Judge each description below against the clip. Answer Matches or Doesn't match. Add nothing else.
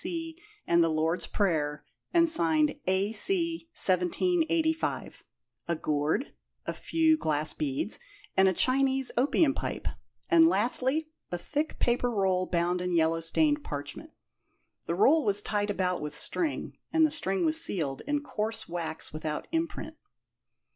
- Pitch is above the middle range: Matches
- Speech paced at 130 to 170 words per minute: Matches